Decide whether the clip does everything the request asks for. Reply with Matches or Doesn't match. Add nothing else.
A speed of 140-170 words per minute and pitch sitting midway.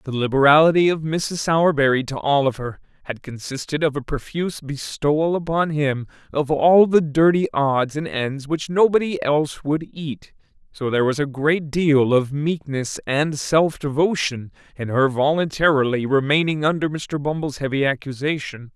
Matches